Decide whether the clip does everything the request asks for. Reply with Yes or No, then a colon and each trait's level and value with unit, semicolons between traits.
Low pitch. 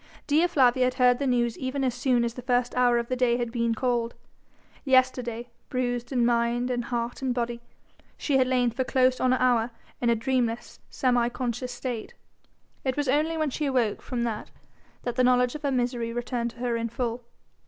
No: high, 245 Hz